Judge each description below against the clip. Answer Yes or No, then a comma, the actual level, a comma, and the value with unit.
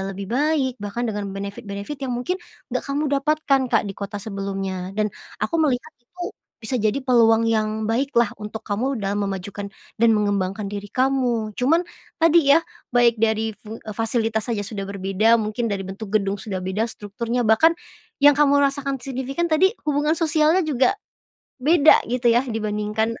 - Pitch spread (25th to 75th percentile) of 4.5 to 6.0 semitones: Yes, average, 4.9 semitones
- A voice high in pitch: Yes, high, 225 Hz